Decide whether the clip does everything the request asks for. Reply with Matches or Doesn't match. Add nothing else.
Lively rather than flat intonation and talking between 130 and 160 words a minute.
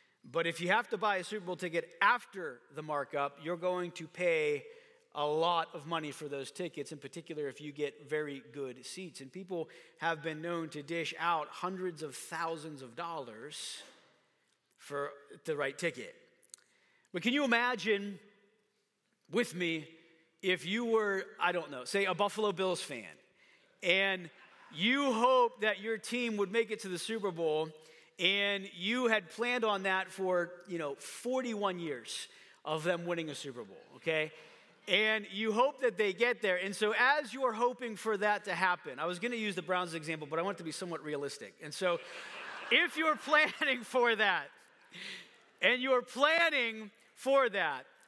Doesn't match